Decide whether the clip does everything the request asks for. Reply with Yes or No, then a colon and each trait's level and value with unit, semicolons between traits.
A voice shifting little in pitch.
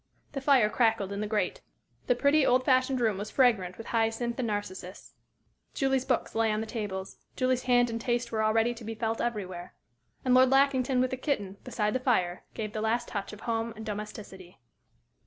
No: average, 3.1 semitones